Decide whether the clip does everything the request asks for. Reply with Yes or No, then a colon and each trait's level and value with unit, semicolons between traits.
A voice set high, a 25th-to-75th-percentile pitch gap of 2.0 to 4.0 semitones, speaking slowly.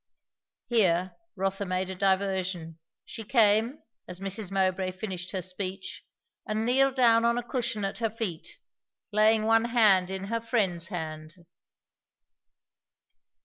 Yes: high, 195 Hz; average, 3.5 semitones; slow, 130 wpm